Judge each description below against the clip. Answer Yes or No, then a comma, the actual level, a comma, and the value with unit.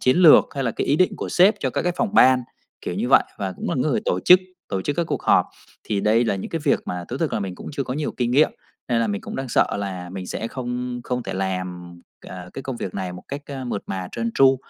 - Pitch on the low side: Yes, low, 120 Hz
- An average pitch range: No, wide, 6.2 semitones